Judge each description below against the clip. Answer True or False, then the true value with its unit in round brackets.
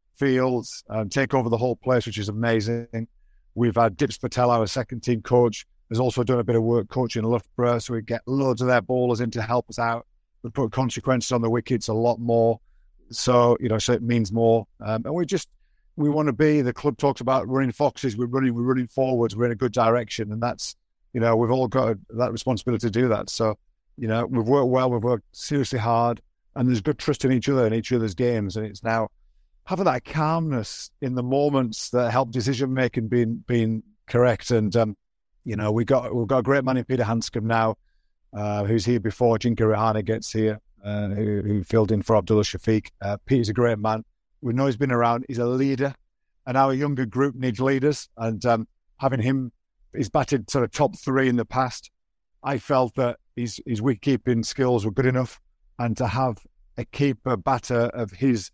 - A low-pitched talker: True (120 Hz)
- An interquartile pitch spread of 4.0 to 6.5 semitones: False (2.5 semitones)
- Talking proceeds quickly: True (215 wpm)